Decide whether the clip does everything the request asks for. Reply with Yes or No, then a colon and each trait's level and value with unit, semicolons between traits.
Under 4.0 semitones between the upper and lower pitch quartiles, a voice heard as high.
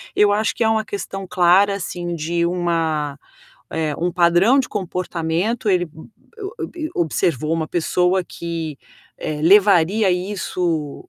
No: average, 3.4 semitones; medium, 175 Hz